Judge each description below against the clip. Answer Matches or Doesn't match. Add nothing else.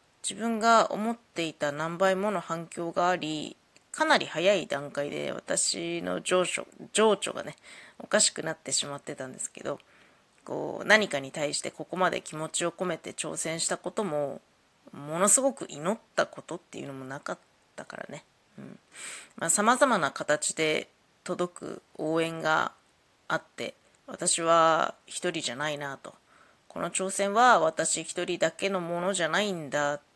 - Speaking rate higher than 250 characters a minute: Matches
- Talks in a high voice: Doesn't match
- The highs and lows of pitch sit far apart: Doesn't match